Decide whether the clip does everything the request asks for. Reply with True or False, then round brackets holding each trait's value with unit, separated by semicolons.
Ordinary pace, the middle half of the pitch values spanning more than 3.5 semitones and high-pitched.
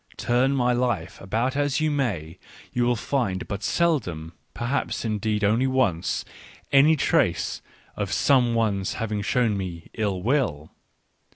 False (150 wpm; 5.1 semitones; 115 Hz)